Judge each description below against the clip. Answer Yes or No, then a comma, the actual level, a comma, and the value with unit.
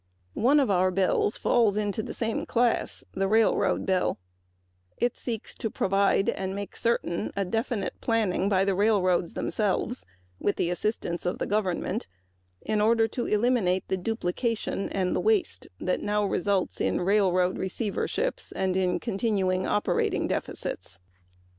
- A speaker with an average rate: No, slow, 125 wpm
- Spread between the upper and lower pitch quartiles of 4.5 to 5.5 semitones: No, average, 3.2 semitones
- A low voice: No, high, 205 Hz